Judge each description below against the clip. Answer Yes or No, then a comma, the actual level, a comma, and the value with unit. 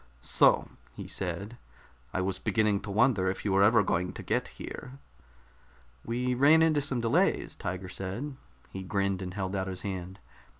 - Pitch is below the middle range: Yes, low, 100 Hz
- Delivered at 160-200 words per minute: Yes, average, 170 wpm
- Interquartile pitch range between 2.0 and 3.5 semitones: No, average, 4.2 semitones